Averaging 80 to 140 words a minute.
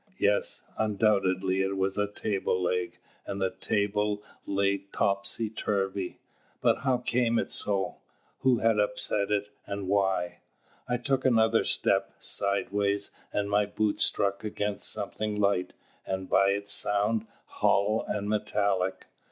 Yes: slow, 135 wpm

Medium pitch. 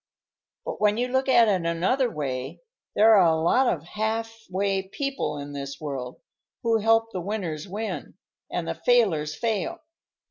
No: high, 200 Hz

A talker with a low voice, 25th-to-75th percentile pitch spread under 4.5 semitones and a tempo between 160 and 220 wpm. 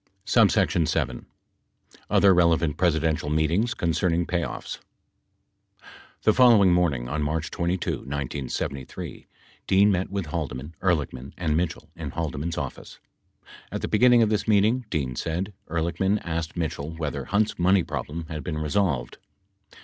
No: very low, 85 Hz; average, 3.8 semitones; slow, 135 wpm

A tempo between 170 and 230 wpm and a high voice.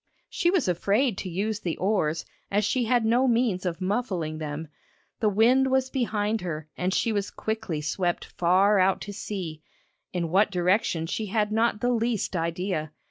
Yes: average, 175 wpm; high, 200 Hz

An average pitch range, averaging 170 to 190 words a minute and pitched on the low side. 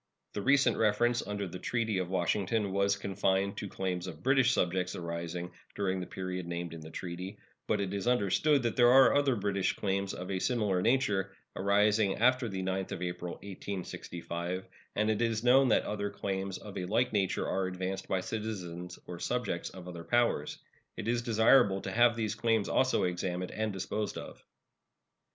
Yes: average, 3.6 semitones; average, 180 wpm; low, 100 Hz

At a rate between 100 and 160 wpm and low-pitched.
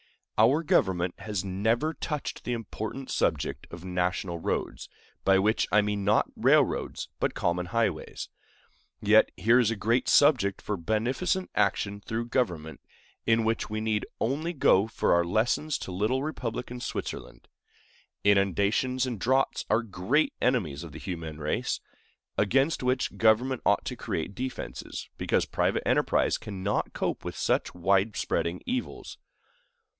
Yes: average, 140 wpm; low, 110 Hz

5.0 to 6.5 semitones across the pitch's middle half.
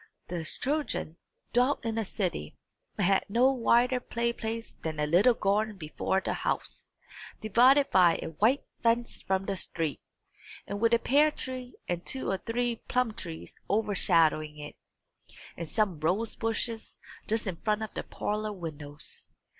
Yes: average, 5.3 semitones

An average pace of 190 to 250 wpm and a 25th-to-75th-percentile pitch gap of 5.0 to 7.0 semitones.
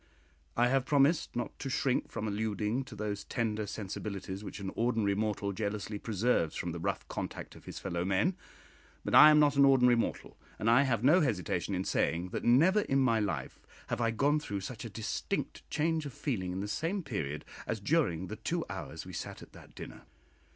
Yes: average, 200 wpm; wide, 5.4 semitones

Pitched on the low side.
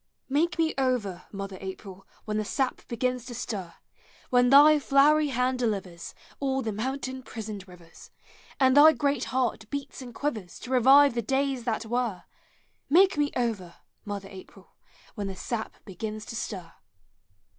No: high, 240 Hz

